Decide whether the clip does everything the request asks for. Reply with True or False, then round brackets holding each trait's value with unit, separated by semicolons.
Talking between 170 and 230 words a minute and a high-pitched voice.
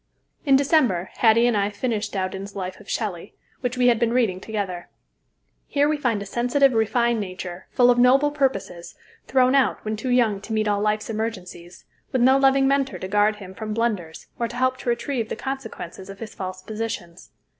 True (195 wpm; 220 Hz)